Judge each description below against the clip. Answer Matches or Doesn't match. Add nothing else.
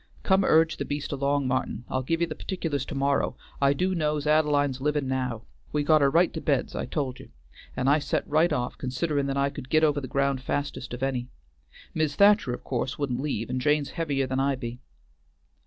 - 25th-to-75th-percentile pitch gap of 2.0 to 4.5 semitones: Matches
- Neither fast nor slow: Doesn't match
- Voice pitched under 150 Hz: Matches